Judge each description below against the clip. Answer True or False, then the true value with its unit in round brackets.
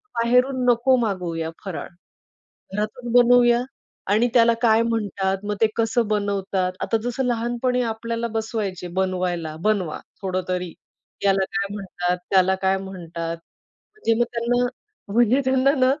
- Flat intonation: False (4.1 semitones)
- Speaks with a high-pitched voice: True (215 Hz)